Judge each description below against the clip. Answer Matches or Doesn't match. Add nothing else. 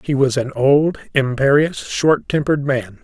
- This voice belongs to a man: Matches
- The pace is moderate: Matches